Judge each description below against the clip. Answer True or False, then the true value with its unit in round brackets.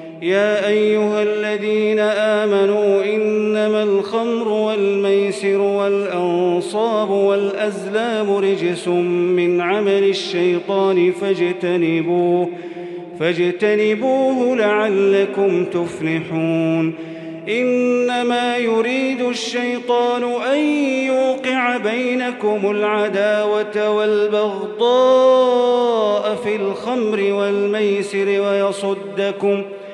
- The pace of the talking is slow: True (60 wpm)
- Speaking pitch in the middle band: False (205 Hz)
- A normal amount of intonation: False (2.0 semitones)